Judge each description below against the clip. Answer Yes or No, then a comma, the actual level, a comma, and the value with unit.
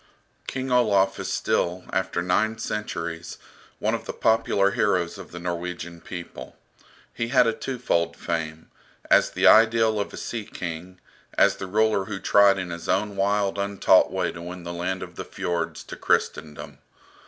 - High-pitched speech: No, very low, 95 Hz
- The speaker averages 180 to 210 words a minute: No, average, 165 wpm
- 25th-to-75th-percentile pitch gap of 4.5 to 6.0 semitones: No, average, 3.6 semitones